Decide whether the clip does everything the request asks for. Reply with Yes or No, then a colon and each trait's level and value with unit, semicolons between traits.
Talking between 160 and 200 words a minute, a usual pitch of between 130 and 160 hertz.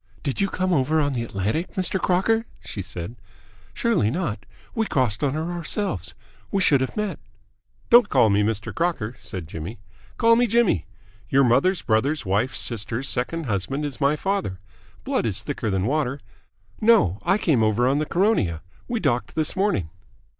Yes: average, 170 wpm; medium, 140 Hz